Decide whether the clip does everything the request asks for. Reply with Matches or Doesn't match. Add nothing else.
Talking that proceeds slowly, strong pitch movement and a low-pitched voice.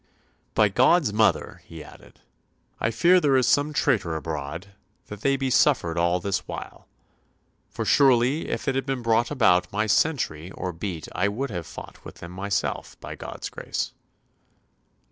Doesn't match